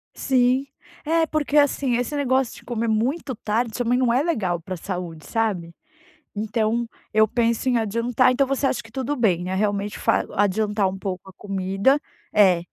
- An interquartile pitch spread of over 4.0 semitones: Yes, average, 4.5 semitones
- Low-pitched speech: No, high, 225 Hz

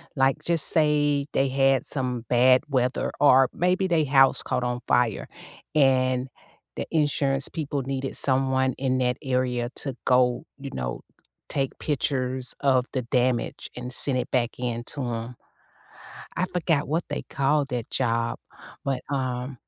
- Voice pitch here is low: Yes, low, 130 Hz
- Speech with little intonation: Yes, narrow, 2.1 semitones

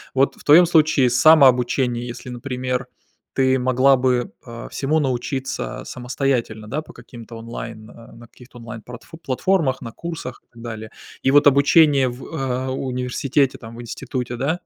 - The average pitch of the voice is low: Yes, low, 130 Hz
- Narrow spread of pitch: Yes, narrow, 2.3 semitones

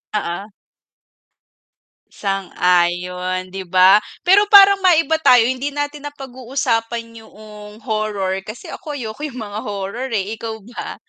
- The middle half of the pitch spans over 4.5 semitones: Yes, average, 5.3 semitones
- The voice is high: Yes, high, 220 Hz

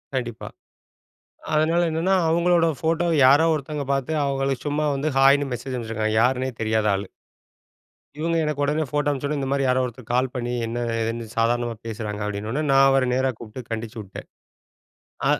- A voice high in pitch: No, low, 135 Hz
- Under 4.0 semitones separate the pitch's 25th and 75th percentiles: No, average, 4.4 semitones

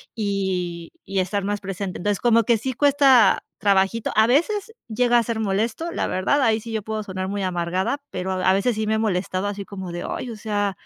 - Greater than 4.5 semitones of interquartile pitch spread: No, average, 3.2 semitones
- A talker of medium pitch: No, high, 205 Hz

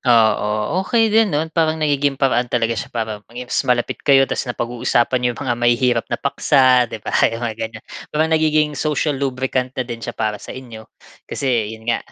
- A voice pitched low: Yes, low, 125 Hz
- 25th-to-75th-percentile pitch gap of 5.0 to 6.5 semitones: No, average, 3.5 semitones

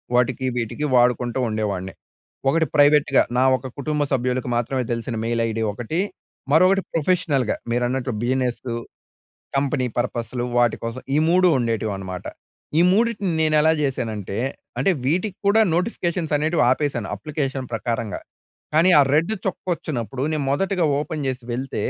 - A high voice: No, low, 130 Hz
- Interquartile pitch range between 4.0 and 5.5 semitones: Yes, average, 4.8 semitones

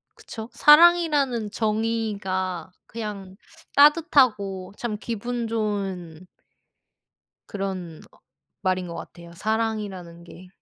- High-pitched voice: Yes, high, 210 Hz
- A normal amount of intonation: Yes, average, 3.7 semitones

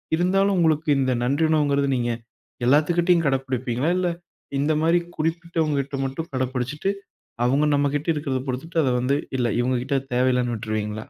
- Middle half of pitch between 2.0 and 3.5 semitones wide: No, average, 4.0 semitones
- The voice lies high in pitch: No, medium, 140 Hz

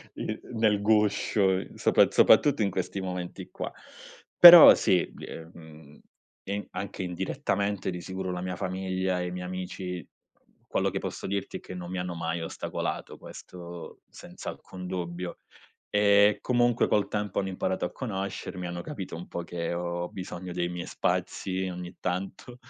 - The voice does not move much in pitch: Yes, narrow, 2.2 semitones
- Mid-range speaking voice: No, very low, 95 Hz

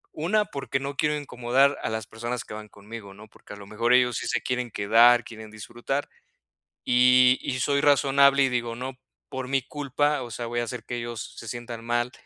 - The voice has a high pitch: No, low, 120 Hz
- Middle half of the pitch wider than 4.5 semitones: No, average, 2.8 semitones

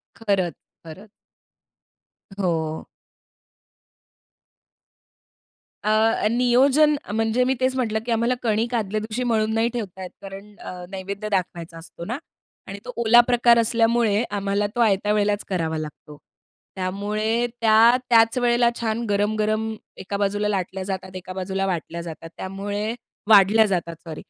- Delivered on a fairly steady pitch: No, average, 3.2 semitones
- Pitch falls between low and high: No, high, 210 Hz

